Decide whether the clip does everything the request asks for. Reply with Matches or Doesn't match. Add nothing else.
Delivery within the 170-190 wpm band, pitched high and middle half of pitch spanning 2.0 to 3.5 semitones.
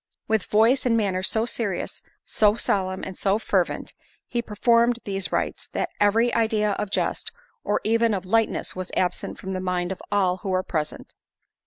Matches